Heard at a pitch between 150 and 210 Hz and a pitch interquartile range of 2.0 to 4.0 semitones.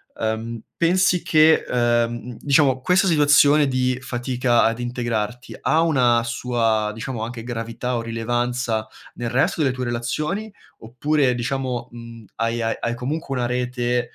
No: low, 120 Hz; narrow, 2.5 semitones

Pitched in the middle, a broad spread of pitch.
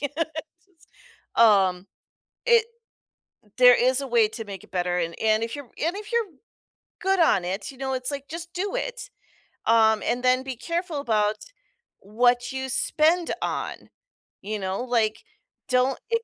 No: very high, 250 Hz; wide, 6.0 semitones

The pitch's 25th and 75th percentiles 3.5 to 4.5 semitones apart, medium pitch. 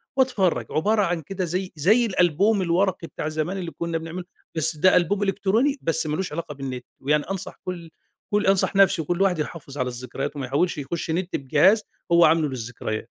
Yes: average, 4.2 semitones; medium, 170 Hz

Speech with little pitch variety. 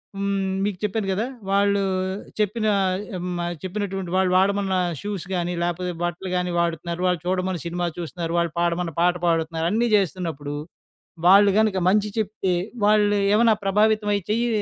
No: average, 3.0 semitones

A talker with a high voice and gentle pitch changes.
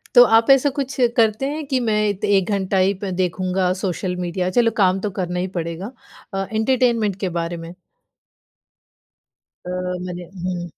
No: high, 195 Hz; average, 3.6 semitones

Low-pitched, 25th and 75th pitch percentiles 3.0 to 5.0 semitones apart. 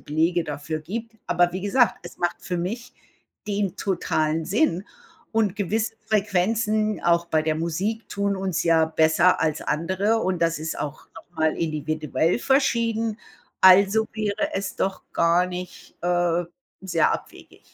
No: medium, 180 Hz; average, 4.3 semitones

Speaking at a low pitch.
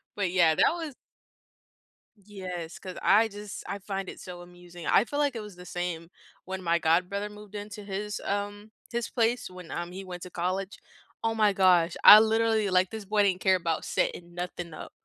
No: high, 190 Hz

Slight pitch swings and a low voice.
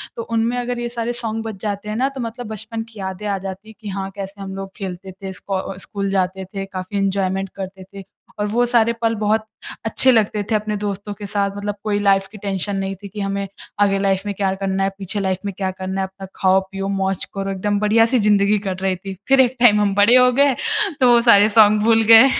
No: narrow, 2.3 semitones; high, 200 Hz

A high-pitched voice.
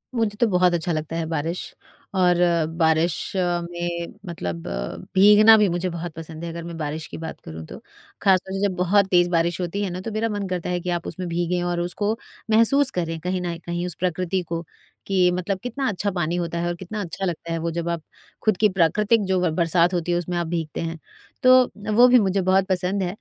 No: medium, 175 Hz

